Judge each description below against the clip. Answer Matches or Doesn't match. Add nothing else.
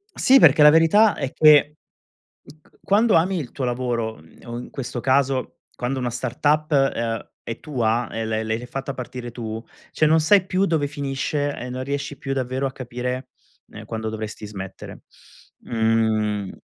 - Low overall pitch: Matches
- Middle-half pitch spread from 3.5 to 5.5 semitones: Matches